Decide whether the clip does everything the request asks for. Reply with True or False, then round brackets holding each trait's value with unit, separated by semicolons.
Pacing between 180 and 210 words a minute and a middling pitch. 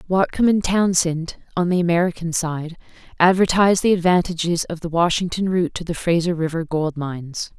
False (160 wpm; 170 Hz)